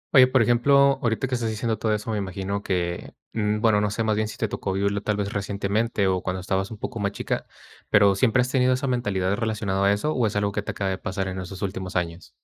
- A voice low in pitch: Yes, low, 105 Hz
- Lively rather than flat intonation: No, average, 2.9 semitones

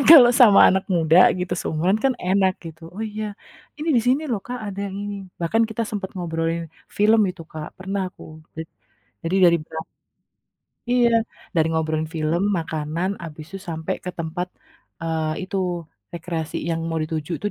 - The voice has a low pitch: No, medium, 175 Hz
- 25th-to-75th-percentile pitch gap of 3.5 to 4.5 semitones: Yes, average, 4.0 semitones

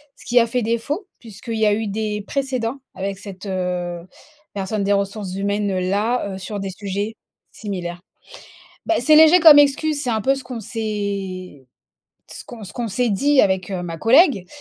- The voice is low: No, high, 210 Hz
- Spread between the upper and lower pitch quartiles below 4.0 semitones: No, average, 4.3 semitones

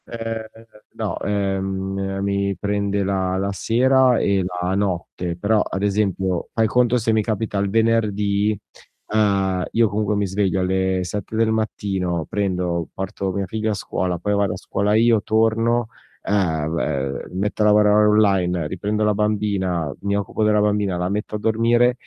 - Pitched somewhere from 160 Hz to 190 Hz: No, low, 100 Hz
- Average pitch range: No, narrow, 2.2 semitones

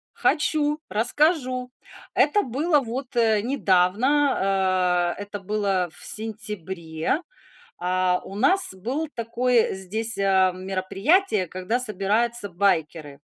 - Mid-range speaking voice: No, high, 210 Hz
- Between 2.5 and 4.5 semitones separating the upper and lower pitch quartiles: No, average, 5.2 semitones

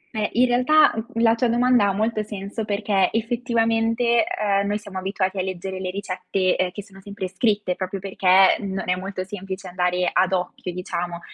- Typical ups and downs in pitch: Yes, average, 3.2 semitones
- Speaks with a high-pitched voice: Yes, high, 200 Hz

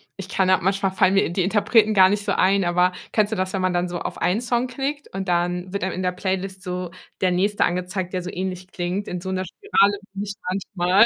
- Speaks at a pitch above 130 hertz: Yes, high, 190 Hz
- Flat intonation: Yes, narrow, 1.8 semitones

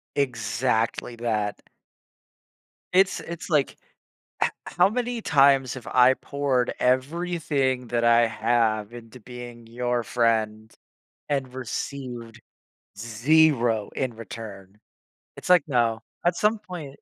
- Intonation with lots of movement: No, average, 3.7 semitones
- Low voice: Yes, low, 125 Hz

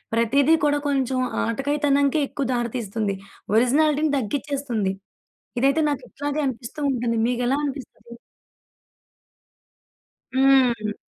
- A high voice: Yes, very high, 265 Hz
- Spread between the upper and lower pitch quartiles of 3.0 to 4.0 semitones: Yes, average, 3.4 semitones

